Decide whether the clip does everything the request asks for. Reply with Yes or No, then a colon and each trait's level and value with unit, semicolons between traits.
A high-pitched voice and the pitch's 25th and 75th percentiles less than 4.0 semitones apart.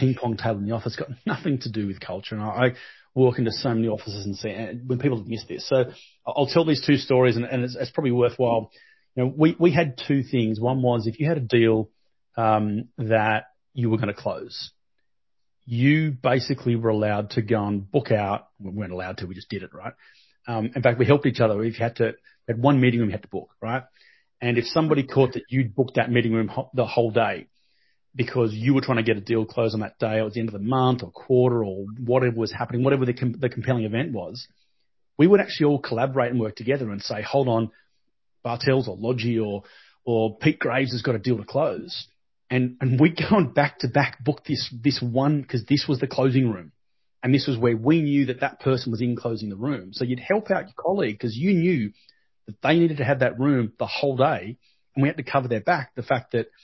No: low, 125 Hz; average, 3.1 semitones